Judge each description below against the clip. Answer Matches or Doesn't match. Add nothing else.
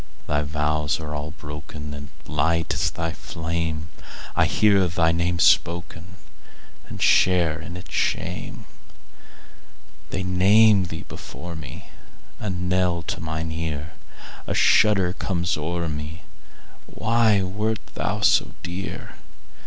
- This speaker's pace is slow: Matches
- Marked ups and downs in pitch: Doesn't match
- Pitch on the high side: Doesn't match